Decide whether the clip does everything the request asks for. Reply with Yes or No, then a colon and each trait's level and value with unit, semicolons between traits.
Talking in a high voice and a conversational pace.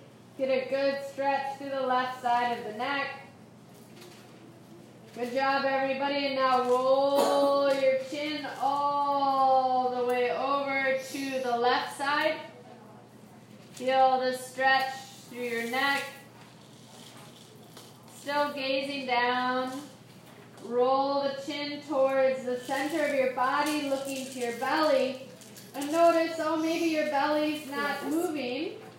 No: very high, 270 Hz; slow, 120 wpm